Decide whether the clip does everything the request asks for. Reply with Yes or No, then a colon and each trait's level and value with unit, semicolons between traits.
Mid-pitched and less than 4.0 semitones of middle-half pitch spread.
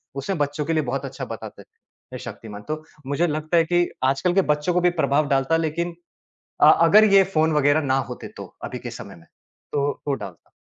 Yes: medium, 150 Hz; average, 3.2 semitones